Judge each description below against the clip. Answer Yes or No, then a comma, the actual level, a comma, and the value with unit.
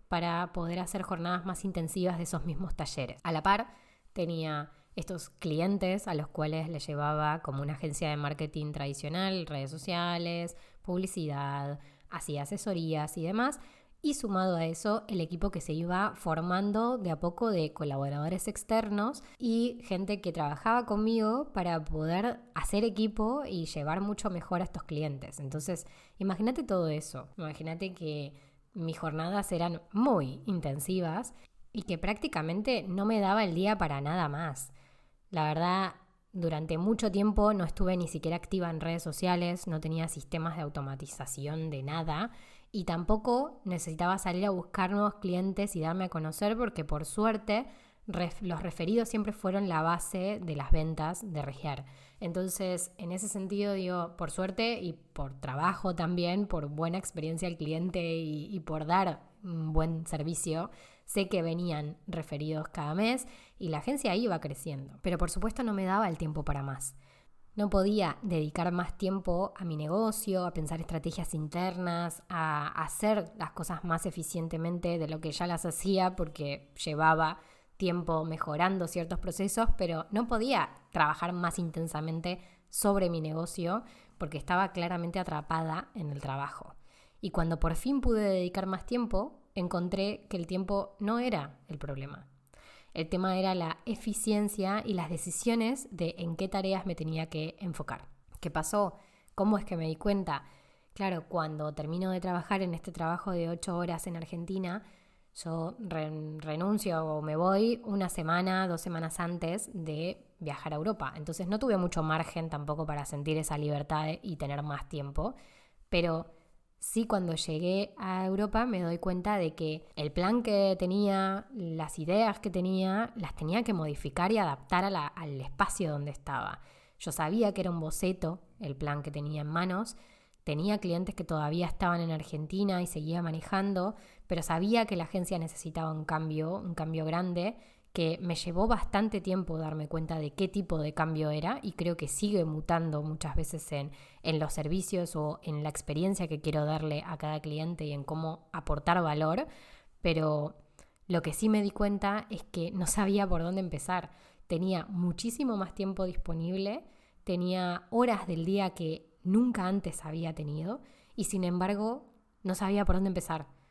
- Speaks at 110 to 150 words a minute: No, average, 165 wpm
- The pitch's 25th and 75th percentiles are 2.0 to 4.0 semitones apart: Yes, average, 3.6 semitones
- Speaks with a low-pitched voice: No, medium, 175 Hz